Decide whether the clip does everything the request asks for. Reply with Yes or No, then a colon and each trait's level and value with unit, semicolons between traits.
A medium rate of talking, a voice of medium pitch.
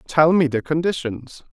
Yes: average, 155 wpm; medium, 150 Hz